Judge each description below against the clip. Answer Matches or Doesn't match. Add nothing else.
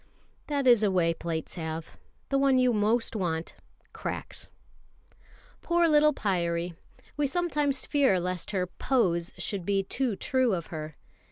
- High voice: Matches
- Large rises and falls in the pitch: Matches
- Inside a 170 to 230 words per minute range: Doesn't match